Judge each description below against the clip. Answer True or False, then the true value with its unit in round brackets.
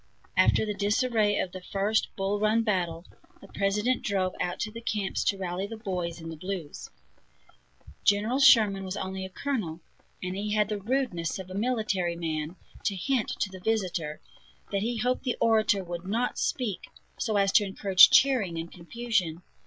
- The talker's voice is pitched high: True (200 Hz)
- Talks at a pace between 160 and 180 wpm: True (175 wpm)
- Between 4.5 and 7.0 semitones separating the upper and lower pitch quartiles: False (3.3 semitones)